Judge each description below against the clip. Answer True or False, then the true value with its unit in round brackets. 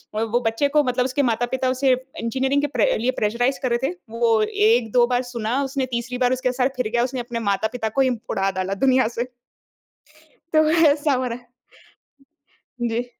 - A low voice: False (245 Hz)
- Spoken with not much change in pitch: True (2.3 semitones)